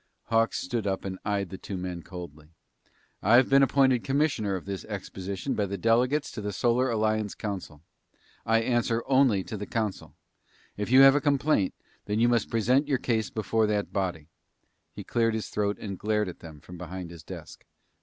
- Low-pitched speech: Yes, low, 105 Hz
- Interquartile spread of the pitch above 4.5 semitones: No, average, 3.9 semitones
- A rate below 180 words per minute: No, average, 185 wpm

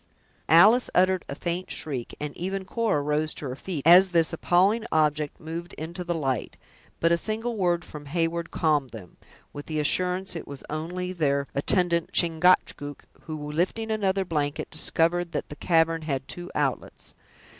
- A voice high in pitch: No, medium, 165 Hz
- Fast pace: No, average, 165 wpm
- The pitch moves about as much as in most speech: Yes, average, 3.4 semitones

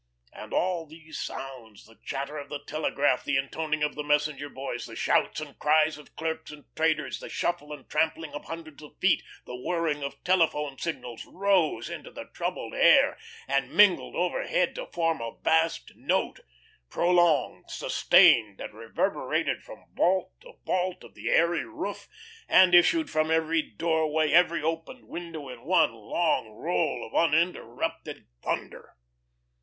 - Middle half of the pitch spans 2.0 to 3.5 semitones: Yes, average, 2.9 semitones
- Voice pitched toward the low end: No, medium, 155 Hz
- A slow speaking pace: No, average, 155 wpm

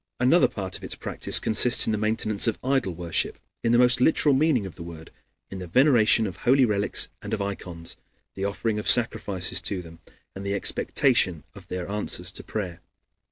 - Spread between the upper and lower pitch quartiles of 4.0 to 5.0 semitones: Yes, average, 4.7 semitones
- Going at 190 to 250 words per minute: Yes, average, 195 wpm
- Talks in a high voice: No, low, 105 Hz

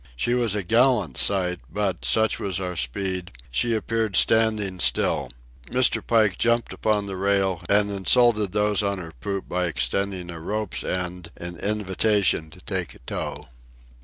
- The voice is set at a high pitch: No, low, 100 Hz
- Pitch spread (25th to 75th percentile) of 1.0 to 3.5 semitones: Yes, average, 3.1 semitones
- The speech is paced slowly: No, average, 160 wpm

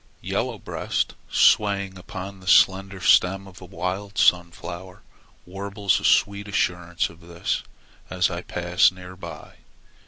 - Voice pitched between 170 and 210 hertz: No, very low, 95 Hz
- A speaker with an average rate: No, slow, 130 wpm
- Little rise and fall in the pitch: Yes, narrow, 1.8 semitones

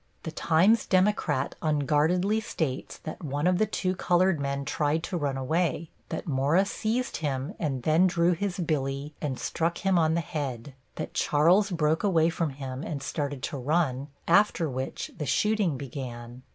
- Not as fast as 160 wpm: No, average, 165 wpm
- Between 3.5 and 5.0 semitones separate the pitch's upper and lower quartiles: Yes, average, 4.3 semitones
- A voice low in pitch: No, medium, 155 Hz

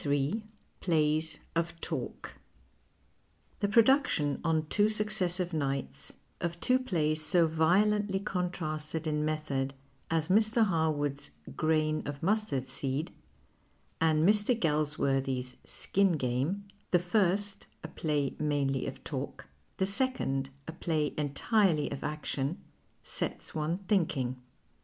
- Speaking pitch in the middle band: Yes, medium, 160 Hz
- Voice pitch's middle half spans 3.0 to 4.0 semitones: No, average, 4.8 semitones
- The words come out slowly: Yes, slow, 120 wpm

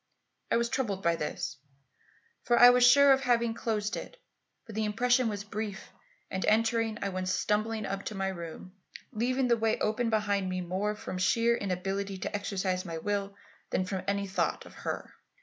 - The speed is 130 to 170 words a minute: No, average, 185 wpm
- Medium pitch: No, high, 210 Hz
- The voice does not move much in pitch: No, average, 3.2 semitones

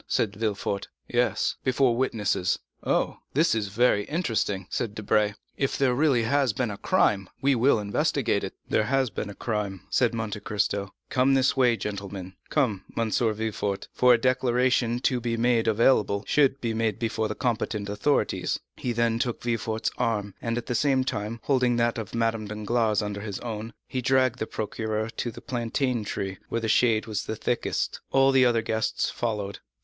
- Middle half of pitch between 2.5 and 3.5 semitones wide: Yes, average, 2.9 semitones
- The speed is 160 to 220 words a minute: Yes, average, 175 wpm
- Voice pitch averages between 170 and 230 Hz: No, low, 115 Hz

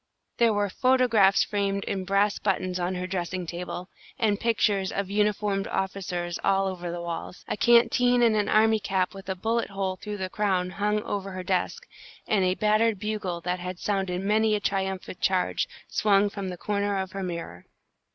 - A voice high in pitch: Yes, high, 195 Hz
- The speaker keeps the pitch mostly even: Yes, narrow, 2.3 semitones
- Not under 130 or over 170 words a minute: No, average, 180 wpm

